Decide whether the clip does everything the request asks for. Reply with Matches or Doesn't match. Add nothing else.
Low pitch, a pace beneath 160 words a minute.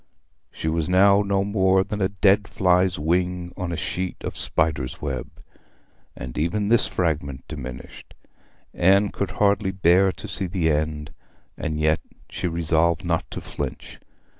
Matches